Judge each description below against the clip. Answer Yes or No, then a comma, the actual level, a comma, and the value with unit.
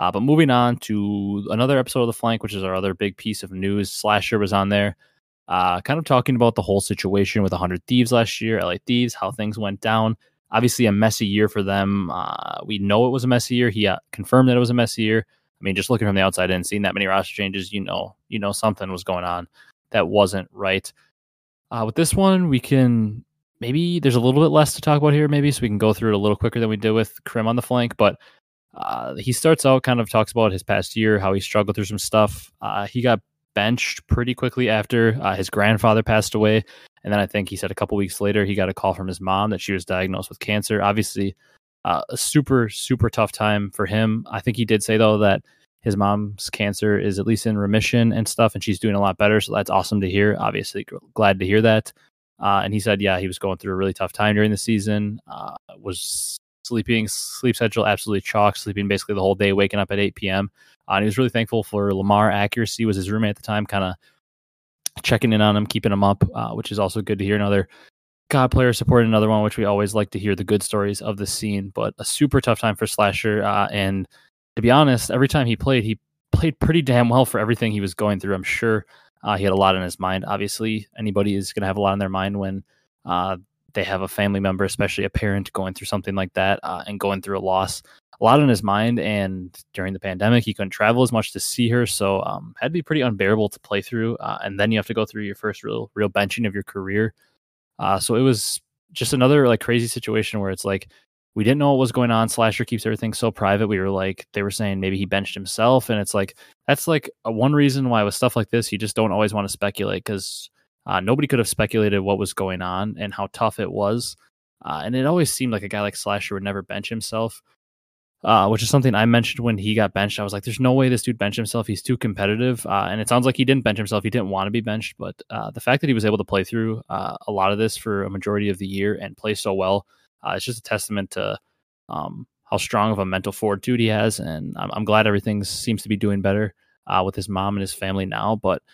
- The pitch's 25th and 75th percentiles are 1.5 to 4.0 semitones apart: Yes, average, 2.8 semitones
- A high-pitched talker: No, low, 105 Hz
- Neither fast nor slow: No, fast, 255 wpm